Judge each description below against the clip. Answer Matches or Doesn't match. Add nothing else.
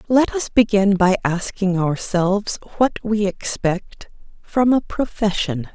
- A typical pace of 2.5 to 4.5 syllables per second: Matches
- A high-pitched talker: Matches